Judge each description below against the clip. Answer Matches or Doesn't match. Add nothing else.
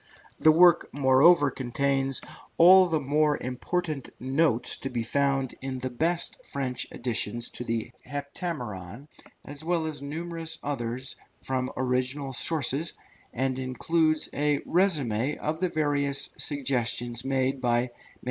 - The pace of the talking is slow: Matches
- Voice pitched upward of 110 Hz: Matches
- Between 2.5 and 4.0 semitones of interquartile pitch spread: Matches